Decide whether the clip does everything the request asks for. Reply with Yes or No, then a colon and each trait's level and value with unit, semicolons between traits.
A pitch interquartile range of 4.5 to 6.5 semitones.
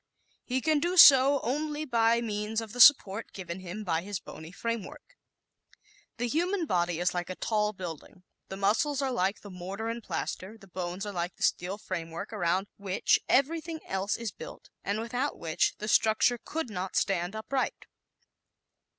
Yes: average, 5.2 semitones